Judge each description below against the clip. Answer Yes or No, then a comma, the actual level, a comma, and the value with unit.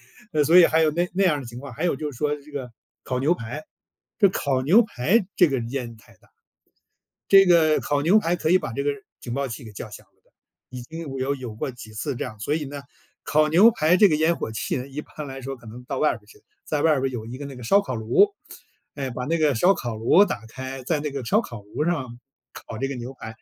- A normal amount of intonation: Yes, average, 4.5 semitones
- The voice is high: No, medium, 140 Hz